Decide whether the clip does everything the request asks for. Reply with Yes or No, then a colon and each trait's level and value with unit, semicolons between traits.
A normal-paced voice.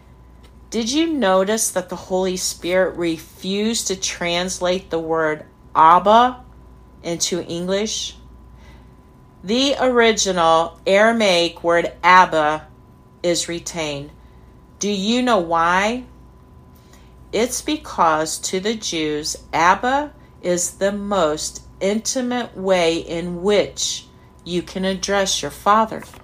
No: slow, 100 wpm